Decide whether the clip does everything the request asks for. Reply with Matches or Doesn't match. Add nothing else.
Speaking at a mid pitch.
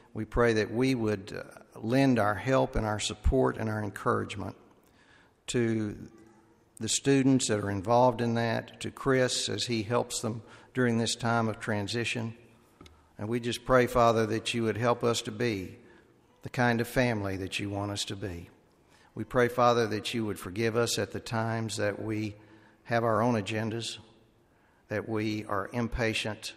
Doesn't match